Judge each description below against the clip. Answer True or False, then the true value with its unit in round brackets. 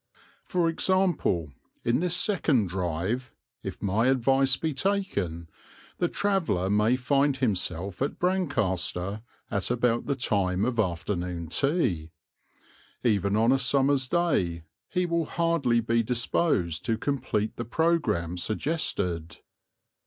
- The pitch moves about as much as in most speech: False (7.8 semitones)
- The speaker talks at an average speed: False (120 wpm)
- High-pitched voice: False (120 Hz)